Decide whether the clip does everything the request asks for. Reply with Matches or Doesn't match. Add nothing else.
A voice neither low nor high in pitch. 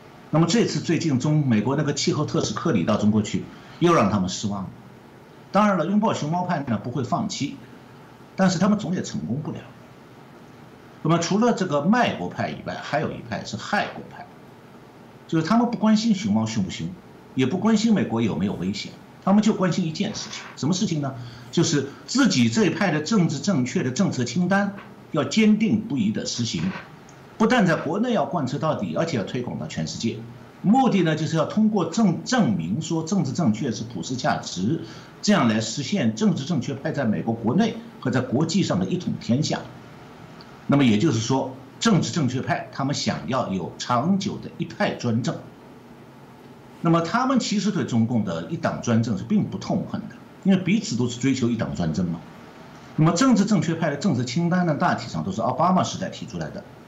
Matches